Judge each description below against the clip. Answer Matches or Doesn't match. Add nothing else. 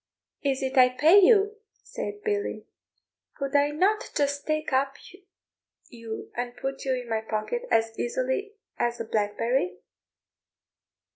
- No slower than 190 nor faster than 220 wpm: Doesn't match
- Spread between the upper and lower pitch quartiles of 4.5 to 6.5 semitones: Matches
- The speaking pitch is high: Matches